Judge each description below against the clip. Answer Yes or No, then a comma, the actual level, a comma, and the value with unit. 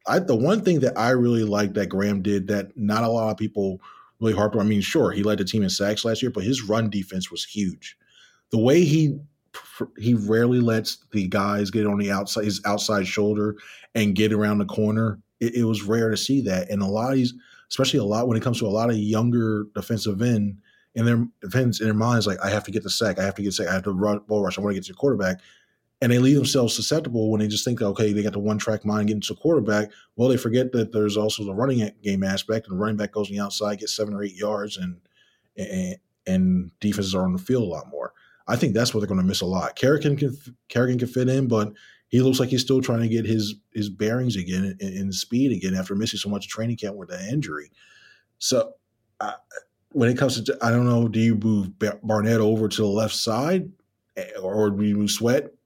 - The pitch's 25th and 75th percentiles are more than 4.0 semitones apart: No, average, 2.8 semitones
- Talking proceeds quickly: Yes, fast, 250 wpm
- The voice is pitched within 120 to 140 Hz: No, low, 110 Hz